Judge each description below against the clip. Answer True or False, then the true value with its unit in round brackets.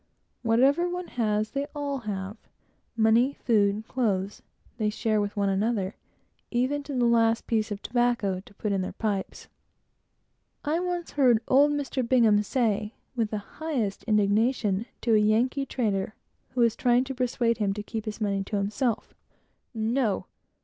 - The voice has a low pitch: False (225 Hz)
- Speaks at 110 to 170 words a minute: True (155 wpm)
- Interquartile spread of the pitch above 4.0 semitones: False (3.5 semitones)